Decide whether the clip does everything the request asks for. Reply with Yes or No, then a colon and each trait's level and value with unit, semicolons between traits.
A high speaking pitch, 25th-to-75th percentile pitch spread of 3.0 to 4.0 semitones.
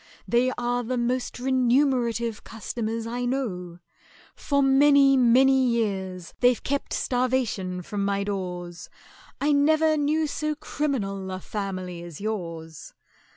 No: high, 235 Hz; wide, 5.5 semitones